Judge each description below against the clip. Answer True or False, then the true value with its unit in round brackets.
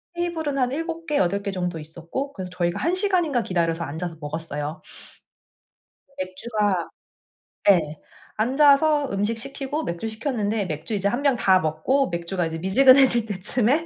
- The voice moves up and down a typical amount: False (8.0 semitones)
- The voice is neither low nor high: False (210 Hz)